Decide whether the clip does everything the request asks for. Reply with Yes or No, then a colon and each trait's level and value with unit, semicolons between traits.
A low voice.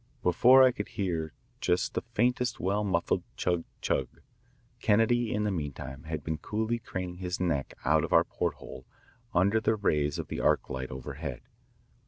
Yes: very low, 90 Hz